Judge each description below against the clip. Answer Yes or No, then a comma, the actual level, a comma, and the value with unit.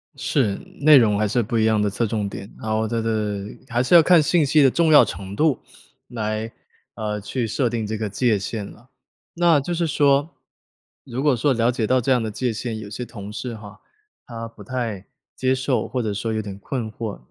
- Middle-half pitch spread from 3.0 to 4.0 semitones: Yes, average, 3.5 semitones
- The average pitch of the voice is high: No, low, 115 Hz